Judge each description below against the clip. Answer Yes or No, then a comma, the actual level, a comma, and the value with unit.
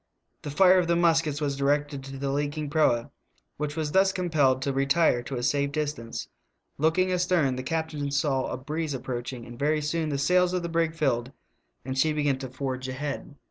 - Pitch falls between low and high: Yes, medium, 145 Hz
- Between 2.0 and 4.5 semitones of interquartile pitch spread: Yes, average, 3.1 semitones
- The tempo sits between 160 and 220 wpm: Yes, average, 200 wpm